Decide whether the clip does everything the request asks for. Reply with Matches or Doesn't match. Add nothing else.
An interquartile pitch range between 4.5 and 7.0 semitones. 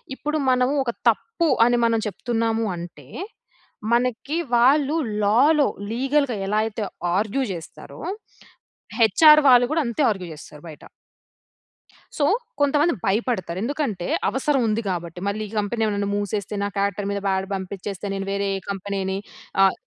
Matches